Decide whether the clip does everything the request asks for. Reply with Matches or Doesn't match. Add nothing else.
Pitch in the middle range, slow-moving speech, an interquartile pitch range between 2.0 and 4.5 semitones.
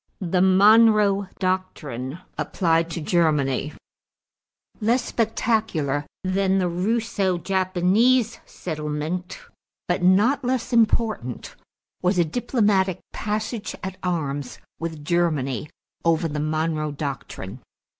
Doesn't match